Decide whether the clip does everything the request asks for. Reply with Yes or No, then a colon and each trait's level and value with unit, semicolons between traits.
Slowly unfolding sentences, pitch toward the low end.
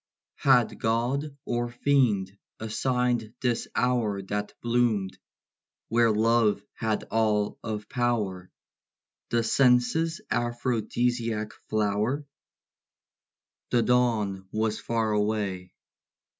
Yes: slow, 90 wpm; low, 115 Hz